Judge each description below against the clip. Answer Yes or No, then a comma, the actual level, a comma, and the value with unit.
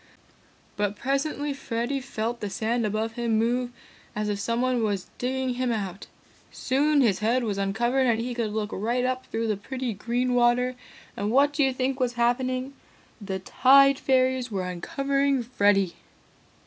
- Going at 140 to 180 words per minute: Yes, average, 160 wpm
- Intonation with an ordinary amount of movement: Yes, average, 3.3 semitones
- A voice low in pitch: No, high, 240 Hz